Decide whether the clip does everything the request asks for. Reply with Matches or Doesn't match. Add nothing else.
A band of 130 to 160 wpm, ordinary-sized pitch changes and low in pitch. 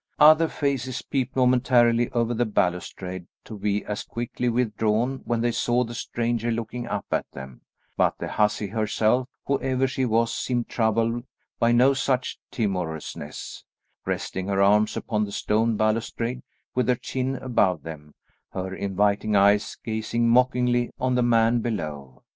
Matches